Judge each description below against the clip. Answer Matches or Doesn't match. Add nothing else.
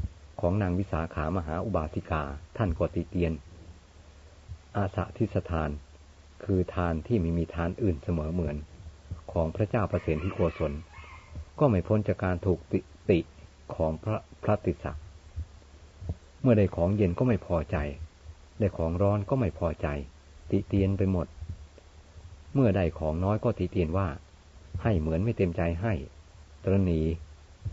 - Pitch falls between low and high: Doesn't match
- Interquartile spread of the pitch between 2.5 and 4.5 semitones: Matches